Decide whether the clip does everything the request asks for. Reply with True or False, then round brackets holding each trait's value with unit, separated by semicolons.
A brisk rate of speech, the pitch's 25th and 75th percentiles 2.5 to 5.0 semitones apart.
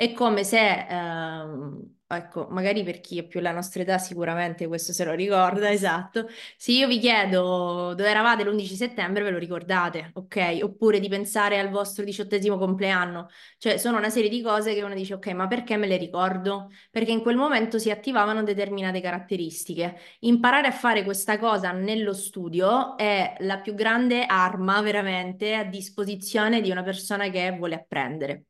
True (175 wpm; 2.9 semitones)